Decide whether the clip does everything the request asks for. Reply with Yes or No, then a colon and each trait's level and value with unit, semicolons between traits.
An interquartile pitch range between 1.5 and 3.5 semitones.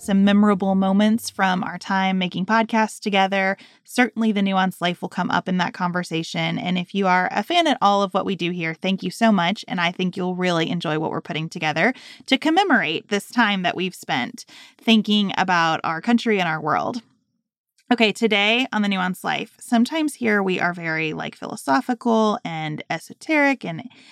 No: average, 4.2 semitones